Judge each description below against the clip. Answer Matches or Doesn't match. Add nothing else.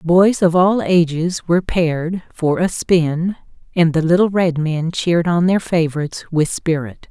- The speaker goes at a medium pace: Matches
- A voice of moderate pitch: Matches